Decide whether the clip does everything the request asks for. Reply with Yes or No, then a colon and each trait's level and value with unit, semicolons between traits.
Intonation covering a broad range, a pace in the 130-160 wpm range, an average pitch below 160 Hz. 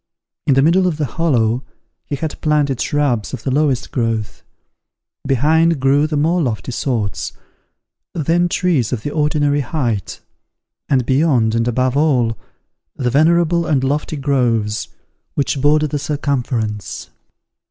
No: average, 3.9 semitones; slow, 135 wpm; medium, 140 Hz